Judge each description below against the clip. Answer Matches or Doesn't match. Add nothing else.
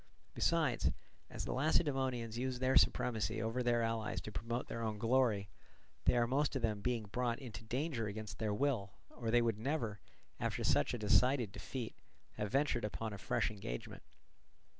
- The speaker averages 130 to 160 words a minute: Doesn't match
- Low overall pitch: Matches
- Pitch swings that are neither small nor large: Matches